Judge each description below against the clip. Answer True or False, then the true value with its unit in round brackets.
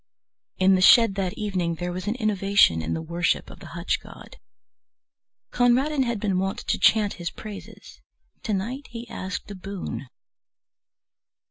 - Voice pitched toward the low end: False (195 Hz)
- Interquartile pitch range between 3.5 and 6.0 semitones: True (3.9 semitones)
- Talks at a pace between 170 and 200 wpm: False (155 wpm)